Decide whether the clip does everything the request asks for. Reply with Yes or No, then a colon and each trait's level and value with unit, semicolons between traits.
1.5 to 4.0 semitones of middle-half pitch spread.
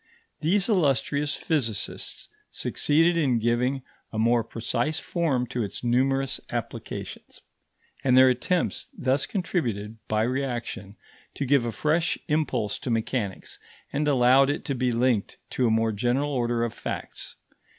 Yes: average, 3.7 semitones